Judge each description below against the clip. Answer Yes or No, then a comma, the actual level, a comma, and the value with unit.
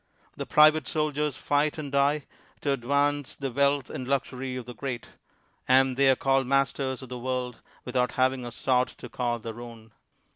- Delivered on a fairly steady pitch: Yes, narrow, 2.1 semitones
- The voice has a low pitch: Yes, low, 130 Hz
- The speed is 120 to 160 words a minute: No, average, 180 wpm